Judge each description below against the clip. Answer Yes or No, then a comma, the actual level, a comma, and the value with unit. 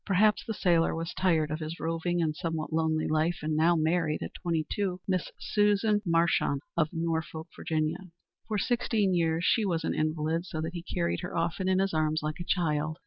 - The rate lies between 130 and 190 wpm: No, average, 200 wpm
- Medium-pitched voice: Yes, medium, 165 Hz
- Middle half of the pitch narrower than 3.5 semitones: Yes, narrow, 2.5 semitones